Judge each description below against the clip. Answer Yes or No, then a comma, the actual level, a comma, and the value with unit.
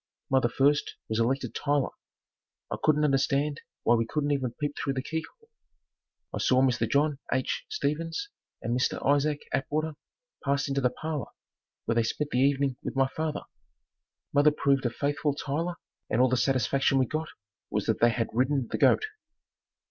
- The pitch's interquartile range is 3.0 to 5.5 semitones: No, narrow, 2.4 semitones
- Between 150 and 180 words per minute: Yes, average, 170 wpm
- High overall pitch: No, medium, 140 Hz